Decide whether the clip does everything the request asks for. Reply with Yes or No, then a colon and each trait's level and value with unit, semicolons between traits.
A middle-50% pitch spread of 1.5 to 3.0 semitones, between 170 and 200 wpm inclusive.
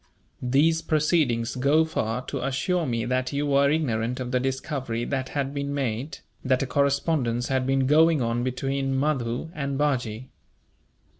No: narrow, 2.6 semitones; average, 155 wpm